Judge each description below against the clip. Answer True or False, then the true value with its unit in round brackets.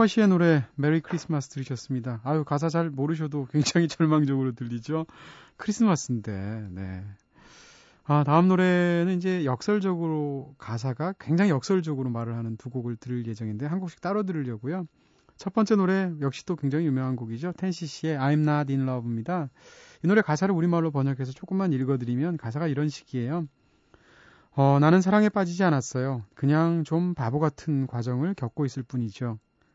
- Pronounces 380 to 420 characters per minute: True (385 characters per minute)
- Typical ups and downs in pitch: True (5.0 semitones)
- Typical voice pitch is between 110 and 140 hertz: False (150 Hz)